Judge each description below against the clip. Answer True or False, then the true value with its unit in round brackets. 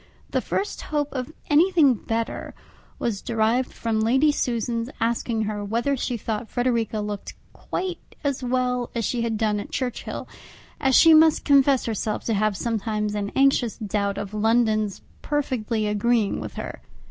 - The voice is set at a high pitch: True (230 Hz)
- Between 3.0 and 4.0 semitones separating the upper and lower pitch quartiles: True (3.4 semitones)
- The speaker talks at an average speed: True (155 wpm)